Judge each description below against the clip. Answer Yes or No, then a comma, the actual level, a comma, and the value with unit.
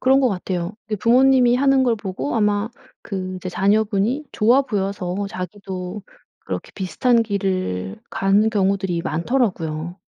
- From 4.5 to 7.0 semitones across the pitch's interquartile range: No, average, 4.1 semitones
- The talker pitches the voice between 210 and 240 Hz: No, high, 200 Hz